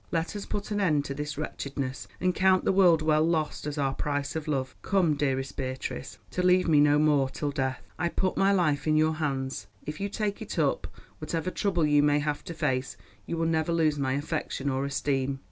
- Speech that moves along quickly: Yes, fast, 215 wpm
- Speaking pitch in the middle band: Yes, medium, 150 Hz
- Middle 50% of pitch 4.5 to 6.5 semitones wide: No, average, 3.4 semitones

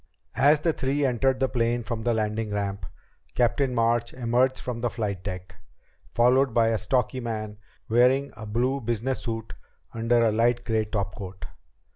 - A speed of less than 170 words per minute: Yes, average, 160 wpm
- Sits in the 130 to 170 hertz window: No, low, 115 Hz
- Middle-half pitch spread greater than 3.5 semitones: No, average, 2.7 semitones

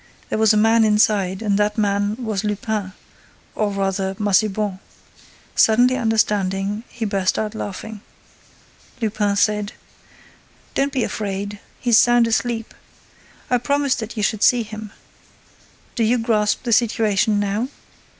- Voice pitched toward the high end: Yes, high, 215 Hz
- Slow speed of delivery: Yes, slow, 130 wpm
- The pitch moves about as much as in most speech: No, narrow, 1.9 semitones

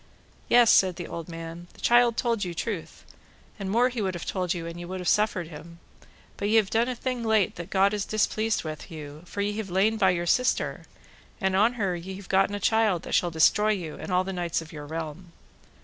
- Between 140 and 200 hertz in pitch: Yes, high, 190 Hz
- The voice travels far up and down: No, average, 4.0 semitones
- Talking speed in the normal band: No, fast, 235 wpm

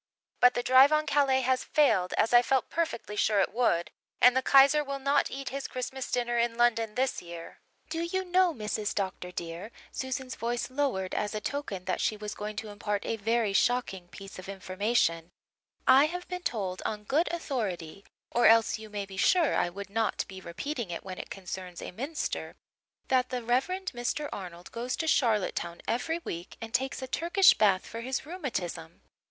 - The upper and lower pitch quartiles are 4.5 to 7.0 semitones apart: Yes, wide, 5.4 semitones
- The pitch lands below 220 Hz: No, high, 235 Hz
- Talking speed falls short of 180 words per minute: No, average, 190 wpm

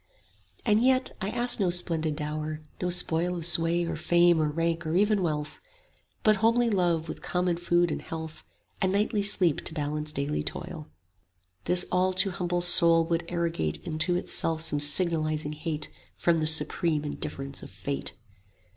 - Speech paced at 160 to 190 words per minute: Yes, average, 165 wpm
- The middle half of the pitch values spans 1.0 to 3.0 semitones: Yes, narrow, 2.5 semitones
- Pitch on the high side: No, medium, 170 Hz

